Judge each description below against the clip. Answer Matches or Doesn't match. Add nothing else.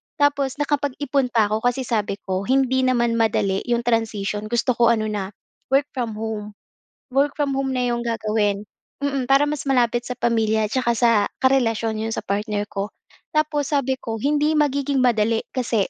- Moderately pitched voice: Doesn't match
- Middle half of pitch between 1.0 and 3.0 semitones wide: Doesn't match